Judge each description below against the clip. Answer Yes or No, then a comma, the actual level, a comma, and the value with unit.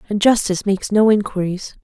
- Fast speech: No, average, 165 wpm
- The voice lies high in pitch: Yes, high, 200 Hz